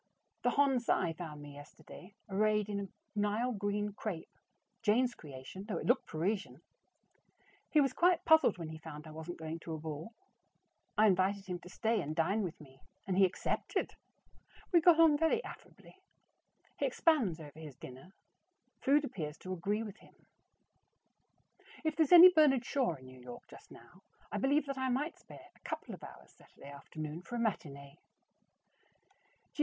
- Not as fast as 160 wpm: No, average, 170 wpm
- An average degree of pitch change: No, wide, 8.2 semitones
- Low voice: No, high, 200 Hz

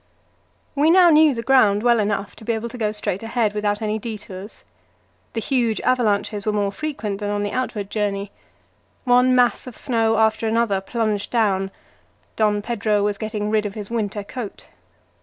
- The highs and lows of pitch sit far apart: No, narrow, 2.4 semitones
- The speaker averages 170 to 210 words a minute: Yes, average, 175 wpm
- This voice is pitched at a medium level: No, high, 215 Hz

